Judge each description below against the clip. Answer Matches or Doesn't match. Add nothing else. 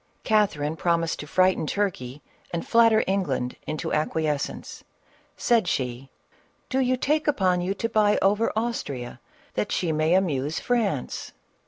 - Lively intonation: Matches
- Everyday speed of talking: Matches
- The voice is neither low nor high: Matches